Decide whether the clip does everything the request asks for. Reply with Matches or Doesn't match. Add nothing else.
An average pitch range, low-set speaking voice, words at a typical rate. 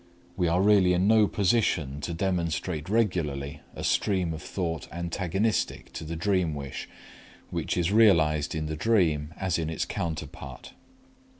Matches